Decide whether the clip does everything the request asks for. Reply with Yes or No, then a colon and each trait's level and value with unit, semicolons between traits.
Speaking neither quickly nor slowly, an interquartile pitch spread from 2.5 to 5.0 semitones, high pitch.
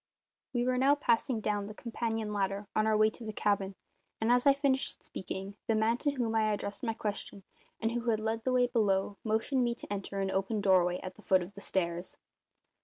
No: fast, 220 wpm; average, 3.1 semitones; high, 215 Hz